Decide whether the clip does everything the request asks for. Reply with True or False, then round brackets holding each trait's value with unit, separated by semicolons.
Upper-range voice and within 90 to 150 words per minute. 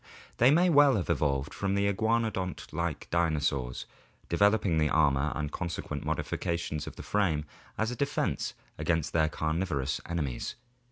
False (85 Hz; 145 wpm)